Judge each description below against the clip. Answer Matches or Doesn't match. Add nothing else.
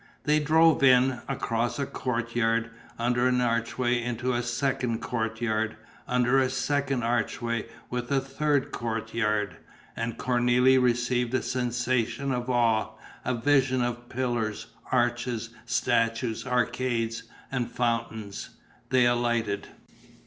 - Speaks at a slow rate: Matches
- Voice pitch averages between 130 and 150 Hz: Doesn't match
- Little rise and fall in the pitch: Matches